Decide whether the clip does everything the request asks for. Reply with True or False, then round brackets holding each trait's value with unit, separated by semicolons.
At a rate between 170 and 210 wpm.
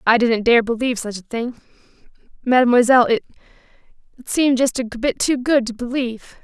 False (150 wpm)